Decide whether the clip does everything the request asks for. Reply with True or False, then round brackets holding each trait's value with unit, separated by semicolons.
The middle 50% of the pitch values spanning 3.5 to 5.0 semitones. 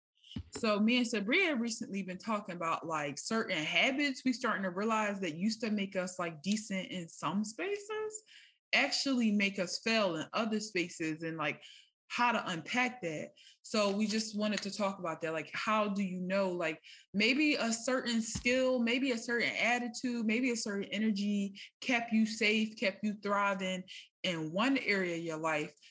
True (4.4 semitones)